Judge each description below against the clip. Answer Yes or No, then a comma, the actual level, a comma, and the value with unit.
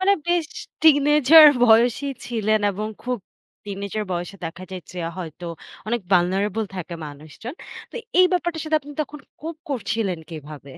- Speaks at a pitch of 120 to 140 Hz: No, high, 220 Hz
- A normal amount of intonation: No, wide, 8.1 semitones